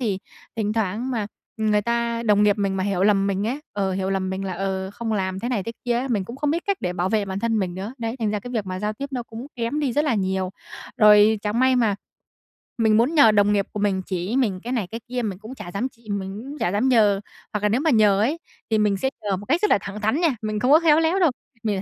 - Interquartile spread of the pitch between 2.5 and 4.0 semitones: Yes, average, 3.6 semitones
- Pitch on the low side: No, high, 215 Hz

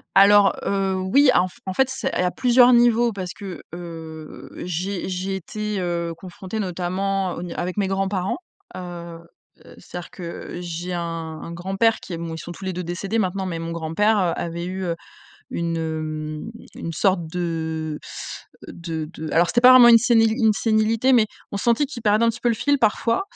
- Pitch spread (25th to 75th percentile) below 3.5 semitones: No, average, 4.2 semitones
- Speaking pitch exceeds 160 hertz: Yes, medium, 185 Hz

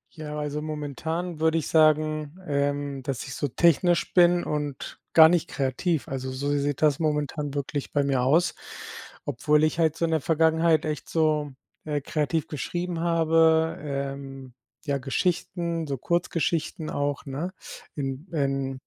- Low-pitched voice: No, medium, 150 Hz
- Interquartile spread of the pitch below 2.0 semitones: No, narrow, 2.6 semitones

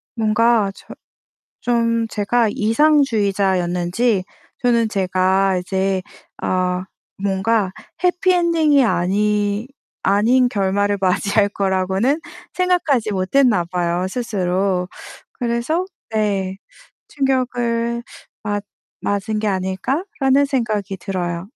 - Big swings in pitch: No, average, 4.2 semitones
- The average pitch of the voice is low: No, high, 210 Hz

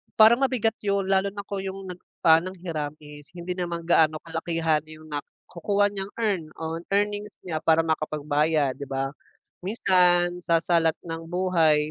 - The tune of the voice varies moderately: Yes, average, 3.5 semitones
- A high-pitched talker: No, medium, 170 Hz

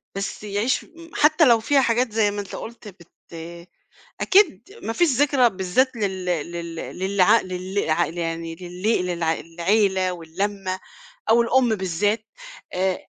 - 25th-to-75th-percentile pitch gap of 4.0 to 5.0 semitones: Yes, average, 4.5 semitones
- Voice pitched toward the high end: Yes, high, 195 Hz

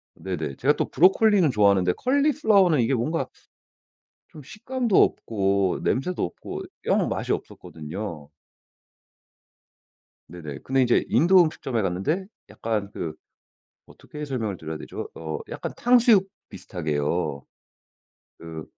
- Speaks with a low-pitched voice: Yes, low, 115 Hz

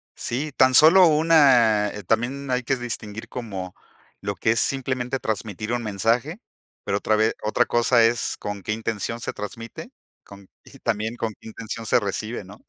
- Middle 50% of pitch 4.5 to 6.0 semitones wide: No, average, 3.1 semitones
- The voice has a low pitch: Yes, low, 115 Hz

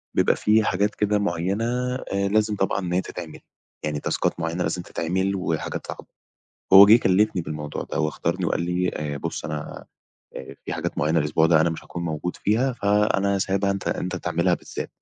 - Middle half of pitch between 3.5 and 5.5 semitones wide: Yes, average, 3.8 semitones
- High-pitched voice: No, very low, 90 Hz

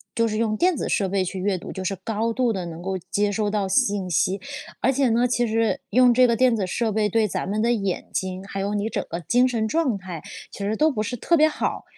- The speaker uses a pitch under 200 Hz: No, high, 215 Hz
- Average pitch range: Yes, average, 3.5 semitones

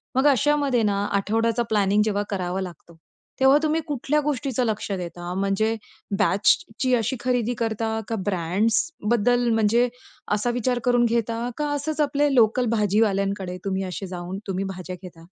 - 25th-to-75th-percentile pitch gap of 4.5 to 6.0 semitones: No, average, 4.0 semitones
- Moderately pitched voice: No, high, 220 Hz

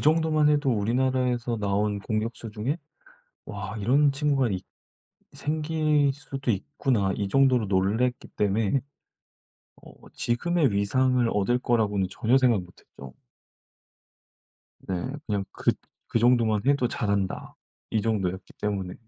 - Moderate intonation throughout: Yes, average, 5.0 semitones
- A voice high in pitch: No, low, 115 Hz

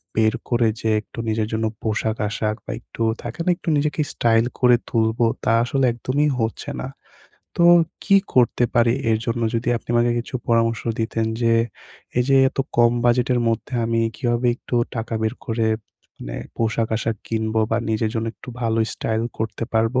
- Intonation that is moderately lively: No, narrow, 1.5 semitones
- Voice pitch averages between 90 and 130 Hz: Yes, low, 115 Hz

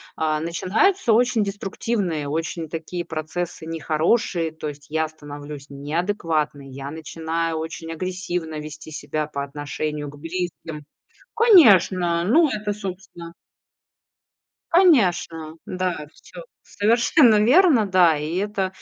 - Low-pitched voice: No, medium, 165 Hz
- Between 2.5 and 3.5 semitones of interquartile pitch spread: No, average, 4.5 semitones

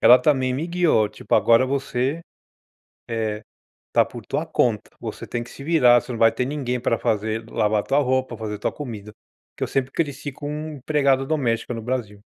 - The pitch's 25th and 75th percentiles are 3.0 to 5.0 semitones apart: Yes, average, 3.9 semitones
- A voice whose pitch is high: No, low, 125 Hz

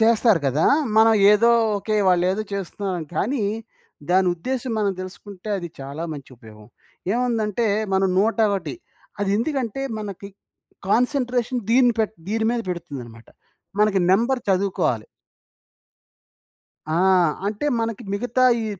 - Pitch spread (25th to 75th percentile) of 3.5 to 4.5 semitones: Yes, average, 4.2 semitones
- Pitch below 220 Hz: Yes, high, 205 Hz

